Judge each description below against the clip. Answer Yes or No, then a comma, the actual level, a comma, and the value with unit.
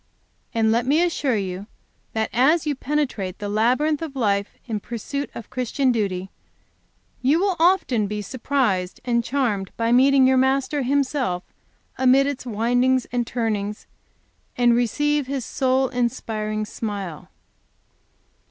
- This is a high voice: Yes, high, 245 Hz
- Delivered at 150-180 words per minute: No, slow, 135 wpm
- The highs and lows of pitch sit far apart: No, average, 4.3 semitones